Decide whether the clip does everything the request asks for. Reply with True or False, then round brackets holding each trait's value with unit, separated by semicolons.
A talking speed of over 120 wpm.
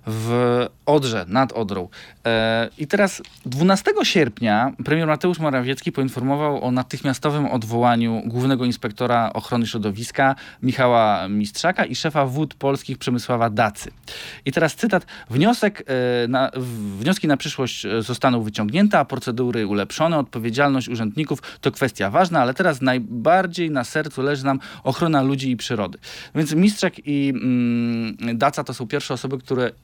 True (140 wpm)